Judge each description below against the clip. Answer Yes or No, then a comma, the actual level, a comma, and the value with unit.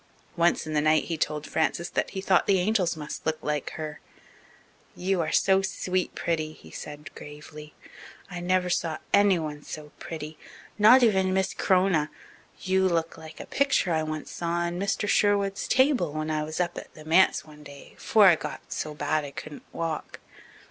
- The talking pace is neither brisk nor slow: Yes, average, 185 wpm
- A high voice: No, medium, 165 Hz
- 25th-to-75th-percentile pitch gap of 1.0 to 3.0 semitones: No, average, 3.6 semitones